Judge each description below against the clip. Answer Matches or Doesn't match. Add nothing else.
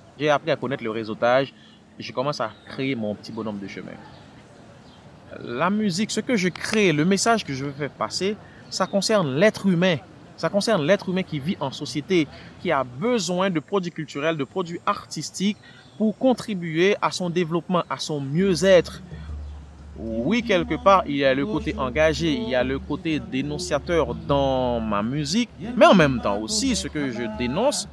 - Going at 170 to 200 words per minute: Matches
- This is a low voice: Doesn't match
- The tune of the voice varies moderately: Doesn't match